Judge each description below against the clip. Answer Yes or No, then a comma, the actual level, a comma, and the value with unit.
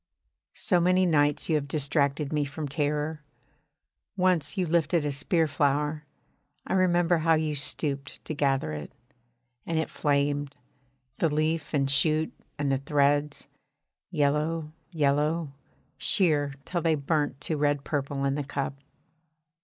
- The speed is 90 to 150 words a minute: Yes, average, 140 wpm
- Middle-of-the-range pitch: Yes, medium, 150 Hz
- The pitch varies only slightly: Yes, narrow, 2.1 semitones